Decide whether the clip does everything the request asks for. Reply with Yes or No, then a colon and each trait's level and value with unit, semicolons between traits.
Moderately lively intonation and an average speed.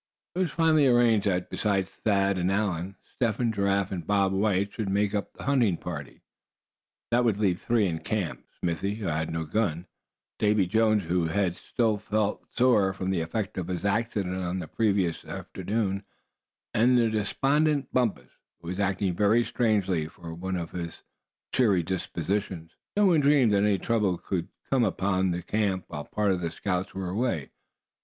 Yes: average, 3.6 semitones; average, 175 wpm